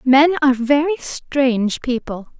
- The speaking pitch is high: Yes, very high, 270 Hz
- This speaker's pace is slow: Yes, slow, 125 wpm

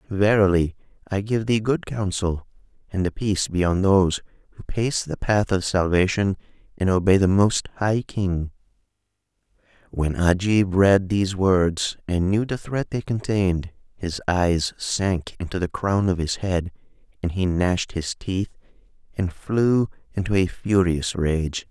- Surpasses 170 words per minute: No, average, 150 wpm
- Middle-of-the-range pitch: No, very low, 95 Hz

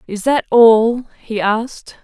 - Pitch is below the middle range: No, high, 230 Hz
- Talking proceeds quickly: No, average, 150 wpm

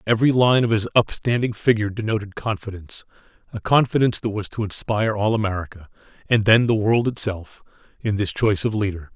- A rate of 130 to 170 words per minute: Yes, average, 165 wpm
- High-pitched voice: No, low, 105 Hz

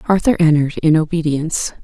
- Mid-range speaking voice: Yes, medium, 160 Hz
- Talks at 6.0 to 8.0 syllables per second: Yes, 6.3 syllables/s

